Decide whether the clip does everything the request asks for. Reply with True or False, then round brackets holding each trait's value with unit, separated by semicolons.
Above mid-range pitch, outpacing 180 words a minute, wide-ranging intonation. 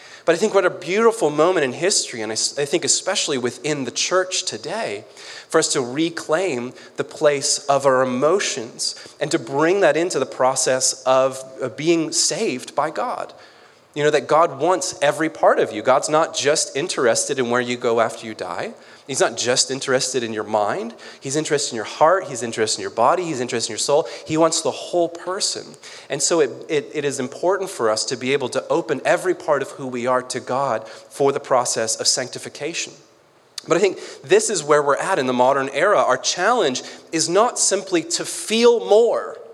False (145 Hz; 200 wpm; 6.2 semitones)